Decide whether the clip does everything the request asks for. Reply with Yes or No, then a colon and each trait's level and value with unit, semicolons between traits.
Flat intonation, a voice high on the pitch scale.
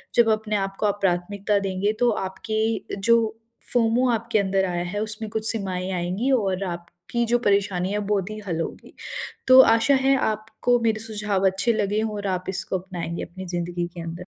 No: average, 3.0 semitones; high, 205 Hz